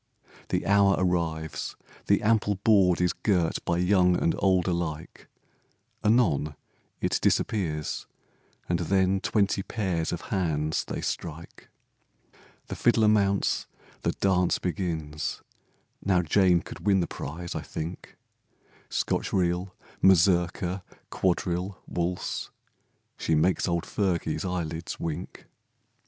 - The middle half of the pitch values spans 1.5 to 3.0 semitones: Yes, narrow, 2.6 semitones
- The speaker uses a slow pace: Yes, slow, 115 wpm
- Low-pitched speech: Yes, very low, 90 Hz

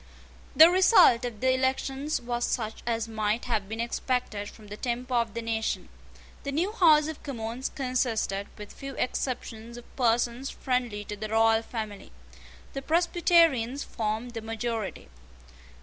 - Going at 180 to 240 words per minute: No, average, 150 wpm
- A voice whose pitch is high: Yes, high, 240 Hz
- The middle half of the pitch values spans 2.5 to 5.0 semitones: Yes, average, 3.2 semitones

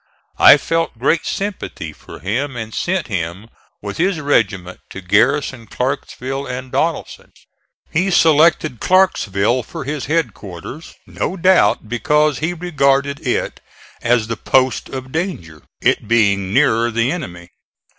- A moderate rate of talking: No, slow, 130 wpm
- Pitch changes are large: Yes, wide, 6.3 semitones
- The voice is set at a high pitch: No, low, 130 Hz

